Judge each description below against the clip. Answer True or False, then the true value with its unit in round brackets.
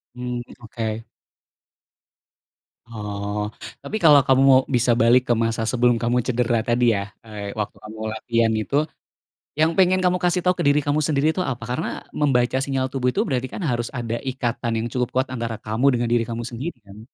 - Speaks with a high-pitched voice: False (120 Hz)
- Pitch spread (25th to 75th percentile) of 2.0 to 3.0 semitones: True (2.7 semitones)